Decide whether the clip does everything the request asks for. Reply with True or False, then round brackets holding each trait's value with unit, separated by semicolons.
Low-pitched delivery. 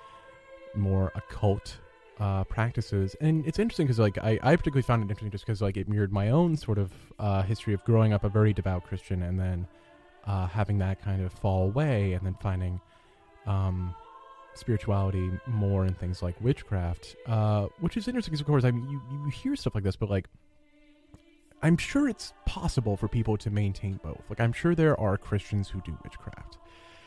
True (105 Hz)